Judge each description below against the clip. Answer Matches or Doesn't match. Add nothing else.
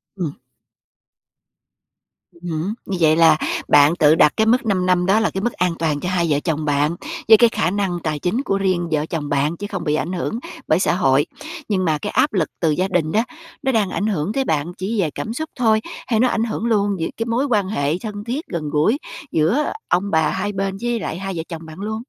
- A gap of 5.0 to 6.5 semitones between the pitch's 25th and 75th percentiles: Matches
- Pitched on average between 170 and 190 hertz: Matches